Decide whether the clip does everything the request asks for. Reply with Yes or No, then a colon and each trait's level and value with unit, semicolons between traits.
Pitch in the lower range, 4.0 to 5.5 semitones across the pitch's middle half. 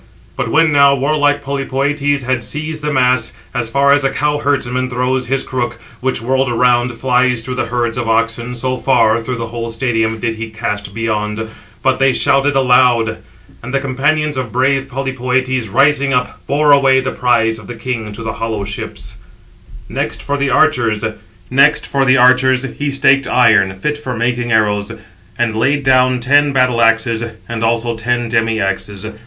No: low, 125 Hz; average, 3.0 semitones